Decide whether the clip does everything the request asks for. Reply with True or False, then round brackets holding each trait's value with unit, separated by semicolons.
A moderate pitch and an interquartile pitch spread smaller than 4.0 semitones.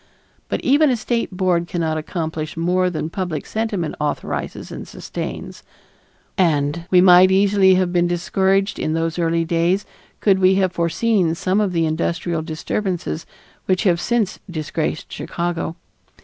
True (175 Hz; 2.5 semitones)